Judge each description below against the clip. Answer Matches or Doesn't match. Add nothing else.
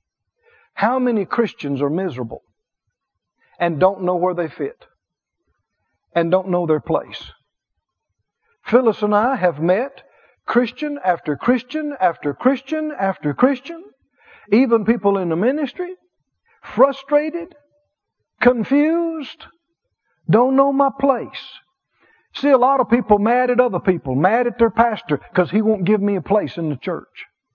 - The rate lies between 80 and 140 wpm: Matches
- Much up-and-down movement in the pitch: Matches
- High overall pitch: Matches